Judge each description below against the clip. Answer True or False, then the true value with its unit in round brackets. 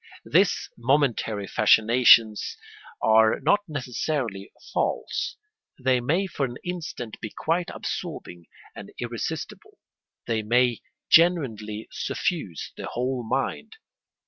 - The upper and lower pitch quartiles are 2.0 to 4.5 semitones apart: False (4.9 semitones)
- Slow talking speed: True (100 wpm)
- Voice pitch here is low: True (125 Hz)